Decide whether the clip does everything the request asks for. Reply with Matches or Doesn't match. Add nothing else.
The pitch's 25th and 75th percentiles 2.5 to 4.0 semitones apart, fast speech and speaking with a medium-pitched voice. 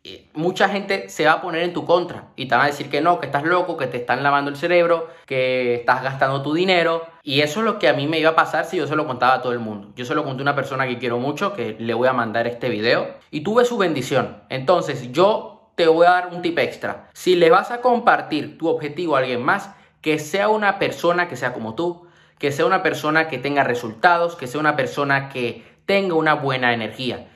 Doesn't match